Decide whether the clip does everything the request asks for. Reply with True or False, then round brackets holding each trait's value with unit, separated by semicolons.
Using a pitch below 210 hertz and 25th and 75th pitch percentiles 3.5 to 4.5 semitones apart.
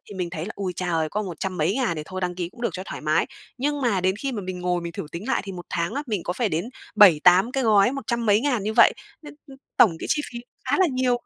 False (195 Hz; 5.1 semitones)